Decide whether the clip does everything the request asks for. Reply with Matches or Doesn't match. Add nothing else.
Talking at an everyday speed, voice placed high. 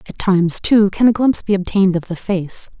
Doesn't match